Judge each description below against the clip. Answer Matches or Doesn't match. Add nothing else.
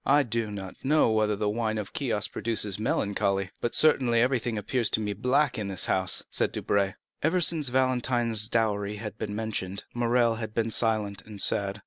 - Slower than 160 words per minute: Doesn't match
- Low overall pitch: Matches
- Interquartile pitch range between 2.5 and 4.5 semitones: Matches